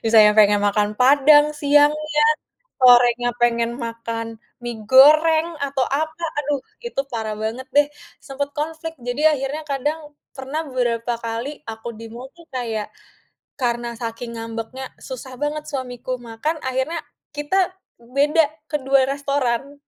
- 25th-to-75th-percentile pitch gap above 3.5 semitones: Yes, average, 4.0 semitones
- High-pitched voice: Yes, very high, 260 Hz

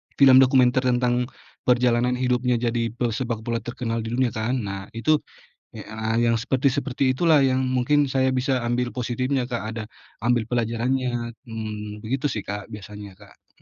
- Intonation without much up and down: Yes, narrow, 2.1 semitones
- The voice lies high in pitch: No, low, 120 Hz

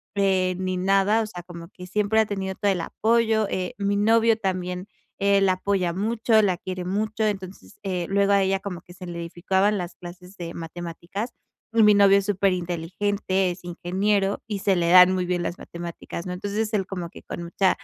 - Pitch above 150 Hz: Yes, high, 190 Hz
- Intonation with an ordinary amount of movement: No, narrow, 2.2 semitones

